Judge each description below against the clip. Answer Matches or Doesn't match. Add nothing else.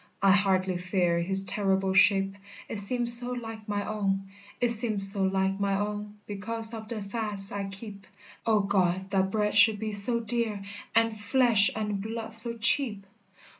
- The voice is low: Doesn't match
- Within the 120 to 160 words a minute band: Doesn't match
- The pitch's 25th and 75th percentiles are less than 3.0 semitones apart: Matches